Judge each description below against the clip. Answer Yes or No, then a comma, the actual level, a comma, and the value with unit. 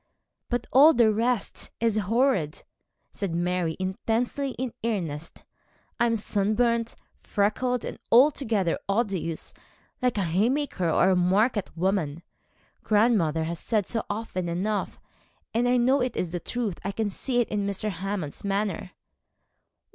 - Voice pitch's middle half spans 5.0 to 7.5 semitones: No, average, 4.6 semitones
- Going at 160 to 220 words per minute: No, average, 140 wpm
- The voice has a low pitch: No, high, 210 Hz